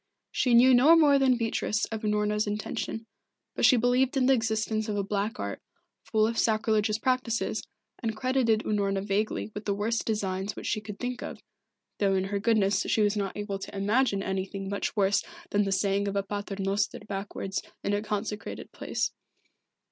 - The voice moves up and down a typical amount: No, narrow, 2.3 semitones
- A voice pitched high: Yes, high, 210 Hz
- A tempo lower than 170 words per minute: No, average, 185 wpm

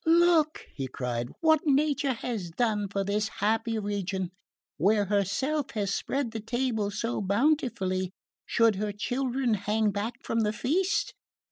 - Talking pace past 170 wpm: No, average, 140 wpm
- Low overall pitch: No, high, 215 Hz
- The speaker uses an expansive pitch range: No, average, 4.3 semitones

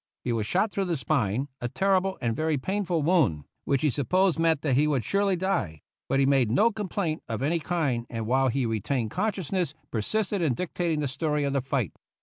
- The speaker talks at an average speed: No, fast, 210 wpm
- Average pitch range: No, wide, 6.5 semitones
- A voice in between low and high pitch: Yes, medium, 150 Hz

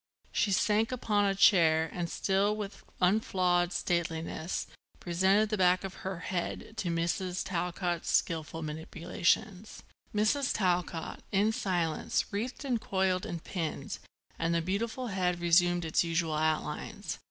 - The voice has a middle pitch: Yes, medium, 180 Hz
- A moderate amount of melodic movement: Yes, average, 3.0 semitones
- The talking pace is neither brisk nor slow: No, slow, 130 wpm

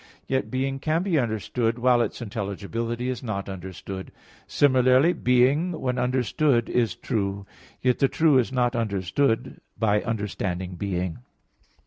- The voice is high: No, low, 120 Hz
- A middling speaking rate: No, slow, 130 wpm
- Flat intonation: No, average, 4.3 semitones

